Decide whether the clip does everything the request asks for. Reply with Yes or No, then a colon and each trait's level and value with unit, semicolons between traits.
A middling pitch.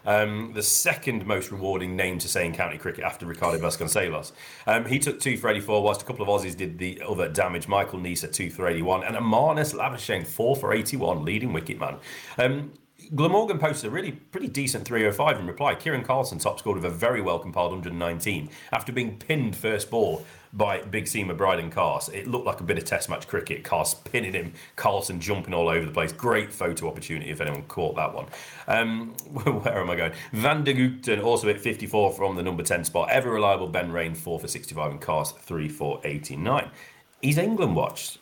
No: low, 105 Hz